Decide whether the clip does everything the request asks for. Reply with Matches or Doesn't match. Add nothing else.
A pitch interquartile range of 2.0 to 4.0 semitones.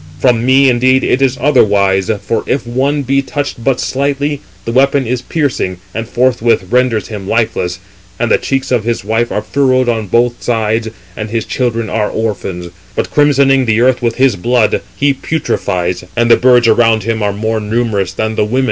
Matches